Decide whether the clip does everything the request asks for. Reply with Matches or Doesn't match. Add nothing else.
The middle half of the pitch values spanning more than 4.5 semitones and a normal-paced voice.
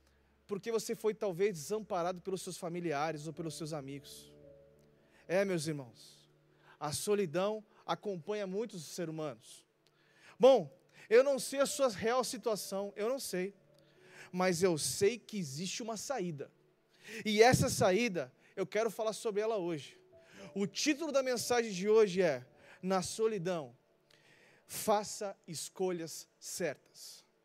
Matches